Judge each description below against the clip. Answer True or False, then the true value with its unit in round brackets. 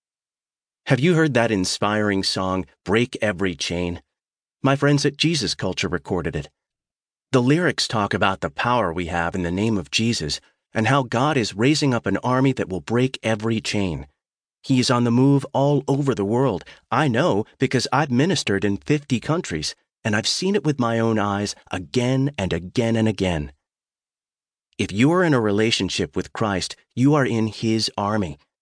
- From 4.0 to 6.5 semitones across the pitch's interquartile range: True (5.5 semitones)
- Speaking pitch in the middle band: False (110 Hz)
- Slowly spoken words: False (180 wpm)